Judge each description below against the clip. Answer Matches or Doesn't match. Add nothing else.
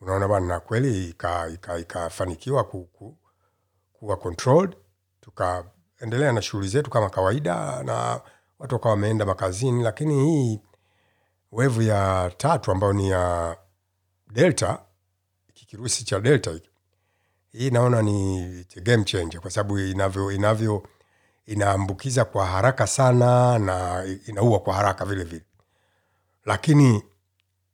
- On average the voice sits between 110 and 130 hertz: Doesn't match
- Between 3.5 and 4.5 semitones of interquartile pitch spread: Matches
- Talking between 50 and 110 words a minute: Matches